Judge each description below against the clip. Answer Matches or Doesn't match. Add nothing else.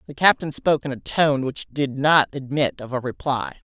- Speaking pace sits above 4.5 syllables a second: Matches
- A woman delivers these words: Matches